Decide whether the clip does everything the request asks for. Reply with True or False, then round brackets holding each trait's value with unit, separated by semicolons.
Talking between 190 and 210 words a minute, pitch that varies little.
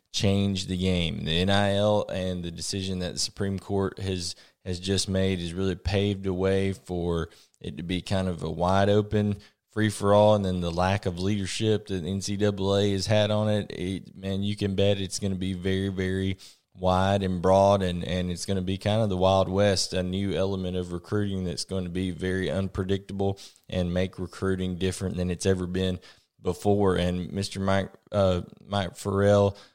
True (195 wpm; 1.5 semitones)